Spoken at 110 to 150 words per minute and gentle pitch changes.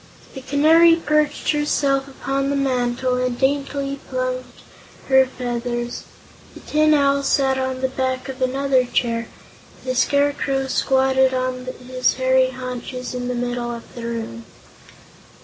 Yes: slow, 135 wpm; narrow, 1.6 semitones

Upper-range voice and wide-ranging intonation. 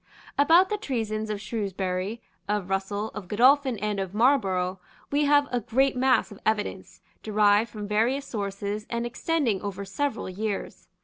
No: high, 215 Hz; average, 4.2 semitones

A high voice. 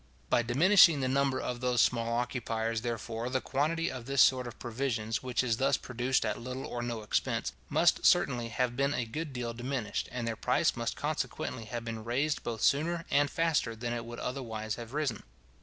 No: low, 125 Hz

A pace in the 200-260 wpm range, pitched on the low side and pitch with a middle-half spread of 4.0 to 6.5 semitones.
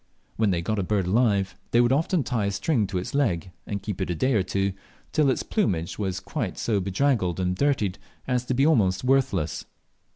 Yes: fast, 205 wpm; low, 100 Hz; wide, 5.6 semitones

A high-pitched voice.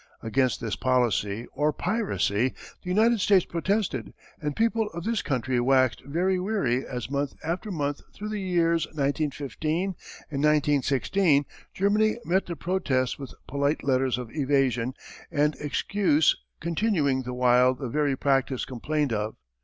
No: medium, 145 Hz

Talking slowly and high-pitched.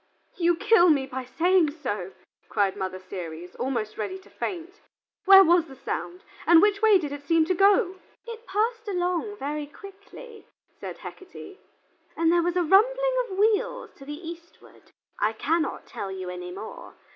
No: average, 170 wpm; very high, 345 Hz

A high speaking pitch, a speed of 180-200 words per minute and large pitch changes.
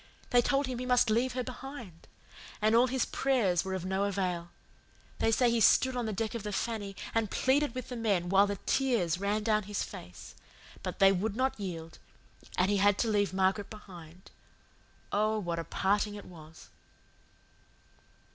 No: high, 210 Hz; average, 185 wpm; average, 4.0 semitones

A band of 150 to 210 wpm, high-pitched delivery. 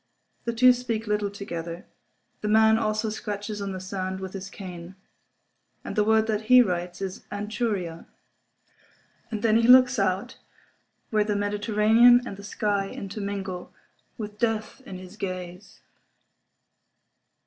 No: slow, 135 wpm; high, 205 Hz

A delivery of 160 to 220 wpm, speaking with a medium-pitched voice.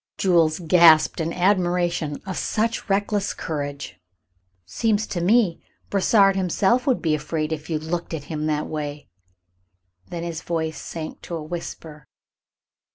No: average, 150 wpm; medium, 170 Hz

